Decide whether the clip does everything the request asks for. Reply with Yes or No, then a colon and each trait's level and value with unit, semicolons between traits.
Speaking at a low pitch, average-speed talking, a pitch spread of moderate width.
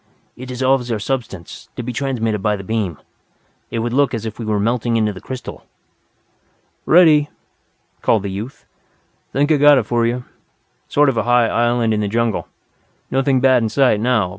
Yes: low, 120 Hz; average, 185 wpm; average, 3.2 semitones